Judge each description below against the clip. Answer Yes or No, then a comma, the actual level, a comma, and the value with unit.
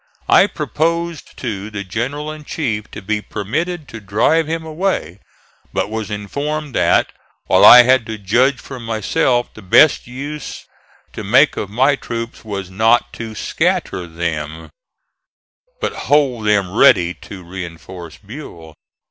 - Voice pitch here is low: Yes, low, 110 Hz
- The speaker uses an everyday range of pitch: No, wide, 6.4 semitones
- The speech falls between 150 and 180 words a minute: No, average, 140 wpm